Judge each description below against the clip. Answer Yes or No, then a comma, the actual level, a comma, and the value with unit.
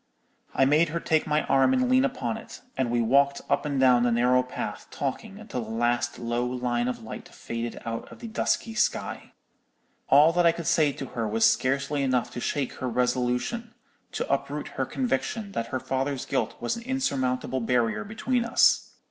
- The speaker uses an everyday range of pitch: No, wide, 6.2 semitones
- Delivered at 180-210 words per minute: Yes, average, 190 wpm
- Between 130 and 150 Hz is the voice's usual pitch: Yes, low, 135 Hz